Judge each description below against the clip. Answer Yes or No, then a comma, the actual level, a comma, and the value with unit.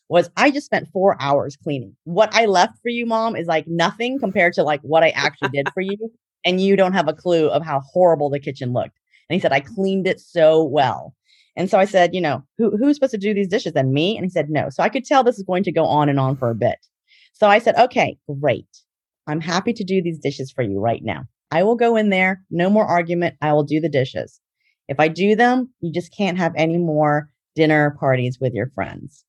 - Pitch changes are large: Yes, wide, 5.7 semitones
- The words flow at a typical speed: No, fast, 250 wpm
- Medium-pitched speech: Yes, medium, 170 Hz